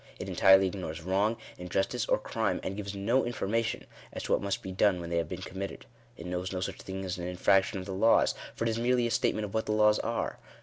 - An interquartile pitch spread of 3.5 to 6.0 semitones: No, narrow, 2.6 semitones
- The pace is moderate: No, fast, 250 wpm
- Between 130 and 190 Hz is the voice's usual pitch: No, very low, 95 Hz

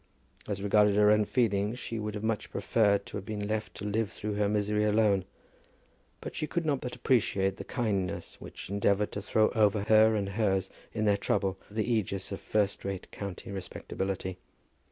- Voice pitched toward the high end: No, low, 105 Hz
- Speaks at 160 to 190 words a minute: Yes, average, 185 wpm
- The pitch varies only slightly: Yes, narrow, 1.6 semitones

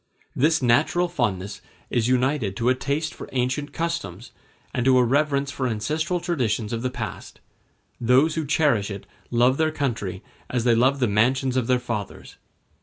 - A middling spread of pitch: Yes, average, 3.7 semitones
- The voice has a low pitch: Yes, low, 130 Hz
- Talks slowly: No, average, 170 wpm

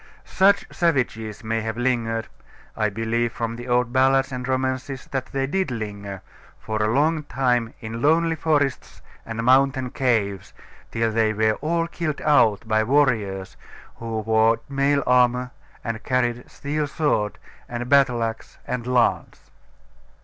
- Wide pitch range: No, average, 3.4 semitones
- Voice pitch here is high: No, low, 125 Hz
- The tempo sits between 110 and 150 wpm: Yes, average, 140 wpm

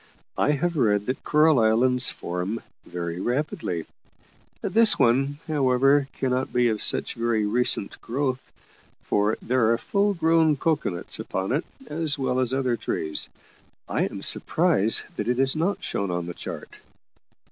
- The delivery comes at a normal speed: Yes, average, 150 wpm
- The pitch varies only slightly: No, average, 5.0 semitones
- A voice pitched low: Yes, low, 125 Hz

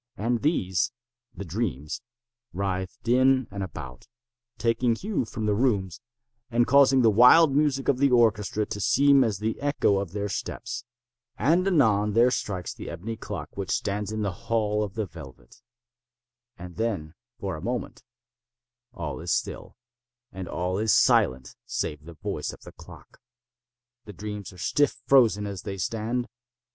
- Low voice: Yes, low, 110 Hz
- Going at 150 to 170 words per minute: Yes, average, 155 wpm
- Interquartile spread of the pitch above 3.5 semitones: Yes, average, 4.2 semitones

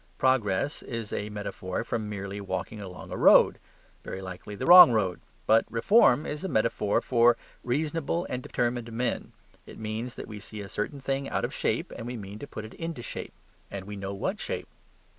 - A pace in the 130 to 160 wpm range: No, average, 195 wpm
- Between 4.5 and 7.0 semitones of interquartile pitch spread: No, average, 3.9 semitones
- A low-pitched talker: Yes, low, 115 Hz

